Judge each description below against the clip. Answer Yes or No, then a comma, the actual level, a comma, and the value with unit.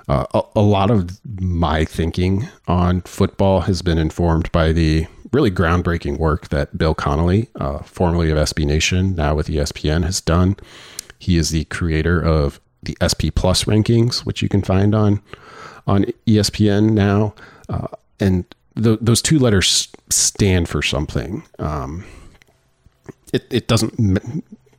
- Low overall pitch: Yes, very low, 90 Hz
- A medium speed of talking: Yes, average, 150 wpm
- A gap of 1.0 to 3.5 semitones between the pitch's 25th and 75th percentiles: No, average, 4.2 semitones